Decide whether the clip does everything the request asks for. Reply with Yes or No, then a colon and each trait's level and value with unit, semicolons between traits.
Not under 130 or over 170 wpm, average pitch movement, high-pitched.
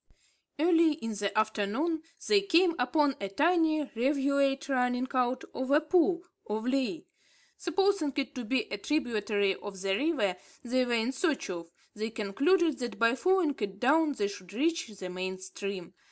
No: average, 165 wpm; wide, 6.9 semitones; very high, 255 Hz